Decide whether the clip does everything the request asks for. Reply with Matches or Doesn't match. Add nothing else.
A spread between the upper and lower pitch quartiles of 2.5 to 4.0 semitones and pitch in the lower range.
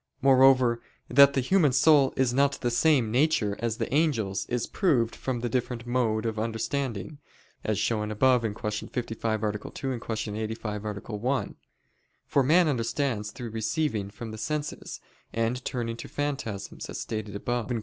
Matches